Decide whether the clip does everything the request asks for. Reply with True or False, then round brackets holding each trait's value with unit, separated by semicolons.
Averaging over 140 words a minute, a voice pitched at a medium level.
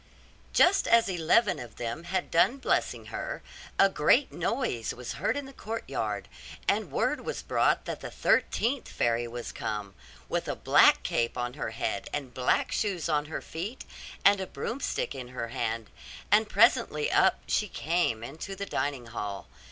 True (165 wpm; 160 Hz)